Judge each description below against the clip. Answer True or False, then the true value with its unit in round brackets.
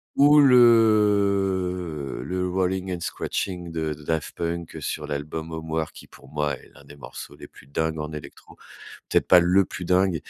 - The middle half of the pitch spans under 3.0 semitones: False (3.3 semitones)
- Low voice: True (85 Hz)